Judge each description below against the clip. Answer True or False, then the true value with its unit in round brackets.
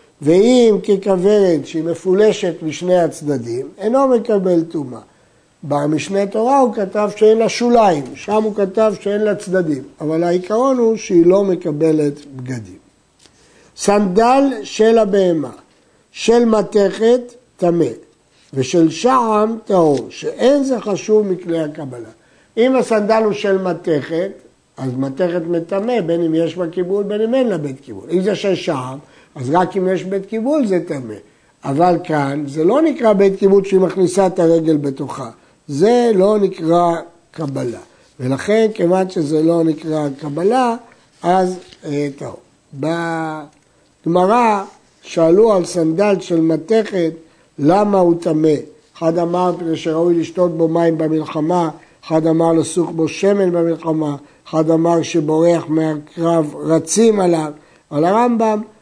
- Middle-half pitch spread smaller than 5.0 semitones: True (4.5 semitones)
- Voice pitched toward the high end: False (175 Hz)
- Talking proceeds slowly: False (135 wpm)